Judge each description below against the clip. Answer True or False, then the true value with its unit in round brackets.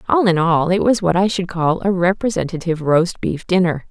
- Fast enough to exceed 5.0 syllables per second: True (5.5 syllables/s)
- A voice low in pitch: False (180 Hz)